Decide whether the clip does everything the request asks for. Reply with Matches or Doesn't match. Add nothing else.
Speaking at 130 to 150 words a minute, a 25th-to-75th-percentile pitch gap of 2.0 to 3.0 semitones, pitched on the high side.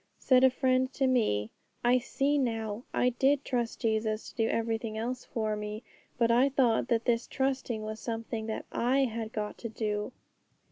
Doesn't match